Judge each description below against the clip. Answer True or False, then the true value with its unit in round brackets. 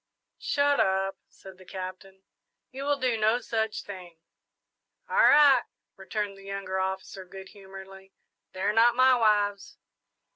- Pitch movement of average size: True (3.4 semitones)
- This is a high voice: True (195 Hz)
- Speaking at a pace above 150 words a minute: False (135 wpm)